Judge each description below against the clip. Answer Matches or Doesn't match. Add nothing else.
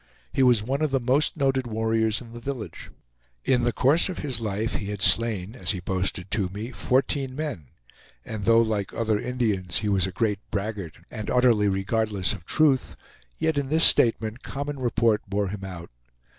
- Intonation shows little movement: Doesn't match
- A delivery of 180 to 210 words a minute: Matches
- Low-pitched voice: Matches